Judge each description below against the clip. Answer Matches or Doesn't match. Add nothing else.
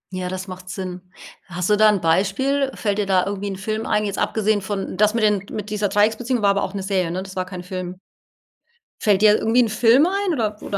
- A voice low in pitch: Doesn't match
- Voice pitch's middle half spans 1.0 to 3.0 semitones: Matches